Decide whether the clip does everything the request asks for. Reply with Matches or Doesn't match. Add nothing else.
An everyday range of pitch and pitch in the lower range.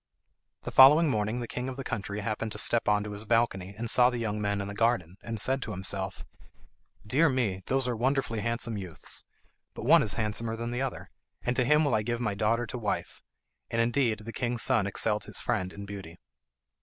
Matches